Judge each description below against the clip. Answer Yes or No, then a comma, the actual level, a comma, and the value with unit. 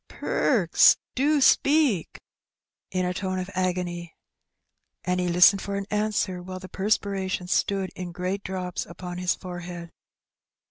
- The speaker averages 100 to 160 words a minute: Yes, slow, 135 wpm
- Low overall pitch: No, medium, 185 Hz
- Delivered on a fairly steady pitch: Yes, narrow, 1.8 semitones